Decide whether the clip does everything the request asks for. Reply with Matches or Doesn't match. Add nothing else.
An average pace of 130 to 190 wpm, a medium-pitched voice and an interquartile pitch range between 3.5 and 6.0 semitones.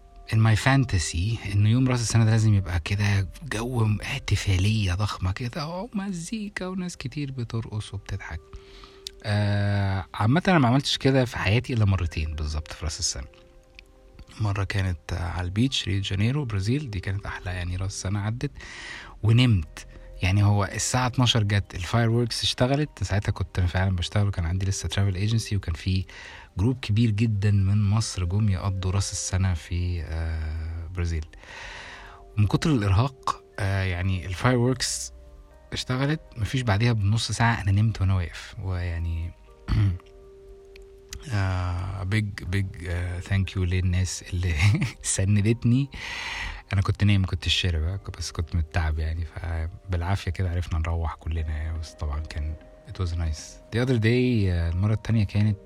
Doesn't match